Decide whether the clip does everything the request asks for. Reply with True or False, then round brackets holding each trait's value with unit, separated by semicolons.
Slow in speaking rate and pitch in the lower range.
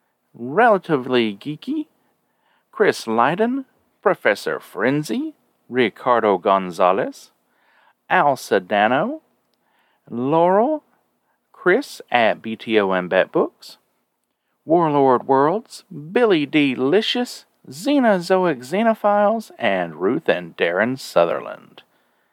False (75 wpm; 175 Hz)